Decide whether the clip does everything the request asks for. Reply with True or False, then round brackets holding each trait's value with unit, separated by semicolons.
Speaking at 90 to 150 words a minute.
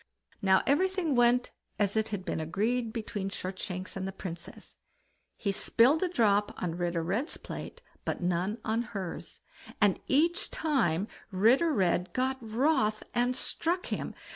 True (145 wpm)